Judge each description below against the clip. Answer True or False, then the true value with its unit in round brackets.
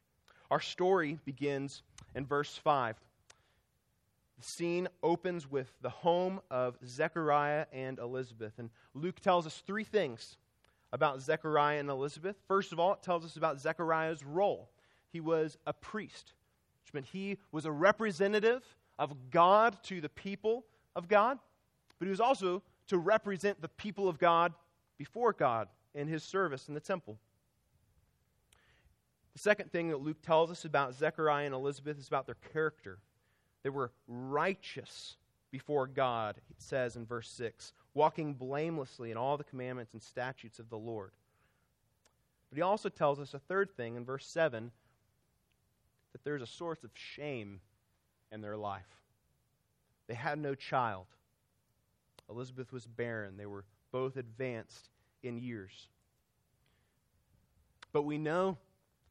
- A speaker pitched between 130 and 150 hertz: True (140 Hz)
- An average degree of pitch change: False (6.2 semitones)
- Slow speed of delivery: False (145 wpm)